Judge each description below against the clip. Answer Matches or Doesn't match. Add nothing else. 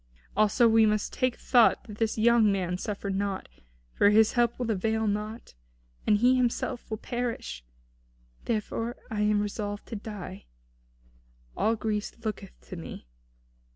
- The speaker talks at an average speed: Matches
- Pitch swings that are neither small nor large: Doesn't match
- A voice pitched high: Matches